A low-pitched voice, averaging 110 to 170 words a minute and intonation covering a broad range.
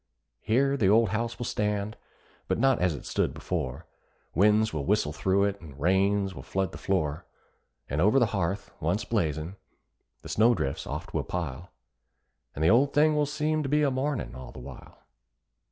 No: low, 100 Hz; average, 185 wpm; wide, 6.6 semitones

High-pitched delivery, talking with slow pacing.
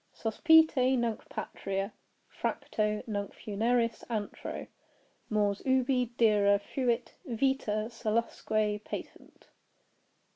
Yes: high, 225 Hz; slow, 80 wpm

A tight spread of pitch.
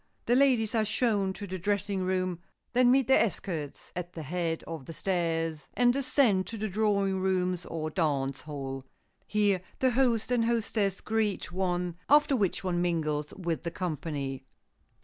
No: average, 4.9 semitones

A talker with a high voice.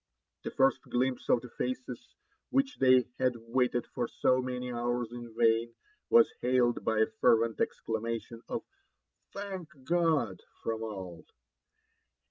No: low, 120 Hz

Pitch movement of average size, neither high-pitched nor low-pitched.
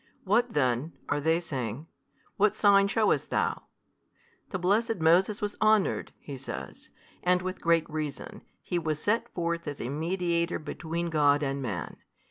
Yes: average, 5.0 semitones; medium, 170 Hz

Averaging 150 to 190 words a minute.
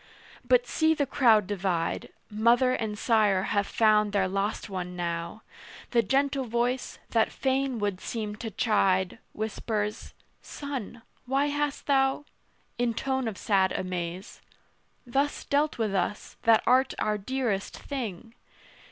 No: slow, 135 wpm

